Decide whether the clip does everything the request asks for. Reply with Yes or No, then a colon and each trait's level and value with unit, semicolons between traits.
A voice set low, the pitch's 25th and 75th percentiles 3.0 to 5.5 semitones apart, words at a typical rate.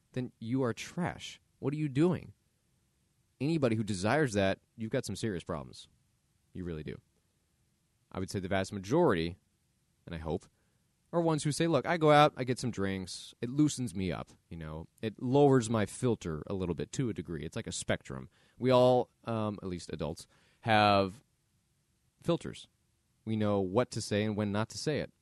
Yes: low, 110 Hz; average, 5.0 semitones; average, 195 wpm